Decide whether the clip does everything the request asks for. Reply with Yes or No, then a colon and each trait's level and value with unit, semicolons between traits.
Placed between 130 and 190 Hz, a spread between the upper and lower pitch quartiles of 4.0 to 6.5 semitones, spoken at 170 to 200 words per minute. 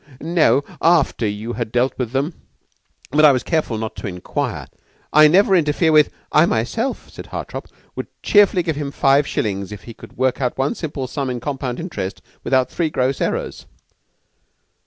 Yes: low, 135 Hz; average, 4.5 semitones; average, 180 wpm